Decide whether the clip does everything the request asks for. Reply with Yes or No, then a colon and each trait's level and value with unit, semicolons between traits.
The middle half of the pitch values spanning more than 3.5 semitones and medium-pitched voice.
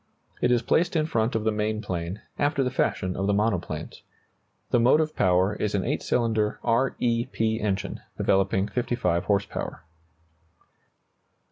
No: average, 3.9 semitones; low, 110 Hz